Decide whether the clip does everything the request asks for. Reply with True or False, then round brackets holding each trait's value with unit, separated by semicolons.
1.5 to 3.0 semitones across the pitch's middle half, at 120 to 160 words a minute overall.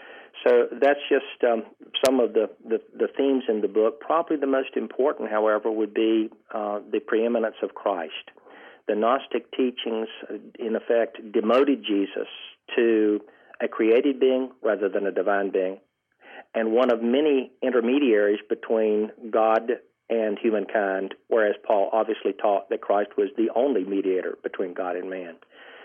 False (4.5 semitones; 150 wpm)